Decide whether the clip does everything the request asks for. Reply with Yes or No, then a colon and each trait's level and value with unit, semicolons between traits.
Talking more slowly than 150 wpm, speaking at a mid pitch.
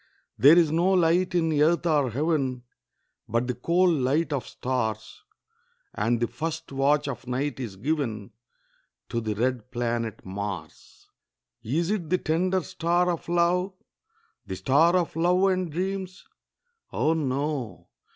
Yes: average, 140 wpm; medium, 150 Hz